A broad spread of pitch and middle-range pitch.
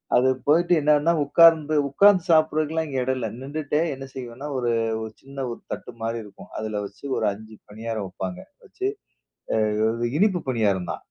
No: wide, 5.9 semitones; low, 130 Hz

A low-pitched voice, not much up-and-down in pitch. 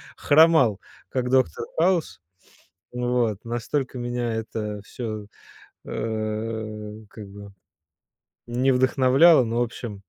No: low, 120 Hz; average, 3.0 semitones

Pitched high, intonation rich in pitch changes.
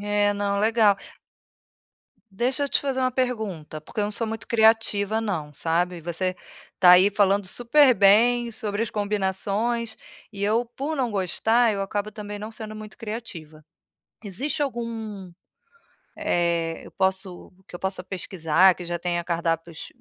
No: high, 205 Hz; average, 3.7 semitones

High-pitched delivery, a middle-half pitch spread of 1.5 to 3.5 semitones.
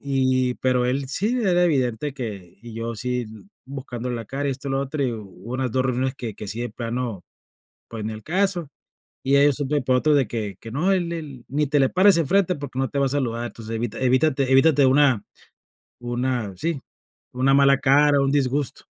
No: low, 130 Hz; average, 3.1 semitones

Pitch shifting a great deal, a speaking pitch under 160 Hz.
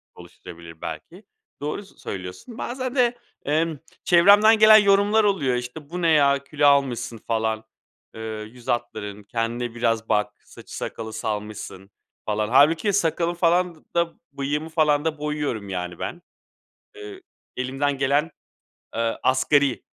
Yes: wide, 7.0 semitones; medium, 140 Hz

